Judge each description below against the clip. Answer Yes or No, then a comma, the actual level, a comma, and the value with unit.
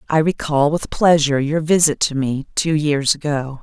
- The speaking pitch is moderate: Yes, medium, 150 Hz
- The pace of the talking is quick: No, average, 180 wpm